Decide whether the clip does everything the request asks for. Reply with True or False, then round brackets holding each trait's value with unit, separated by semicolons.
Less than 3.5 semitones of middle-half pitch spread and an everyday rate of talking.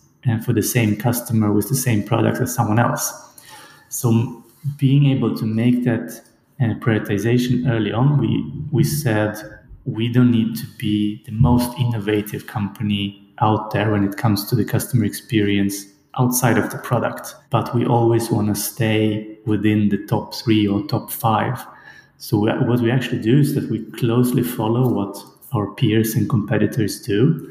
True (2.7 semitones; 165 wpm)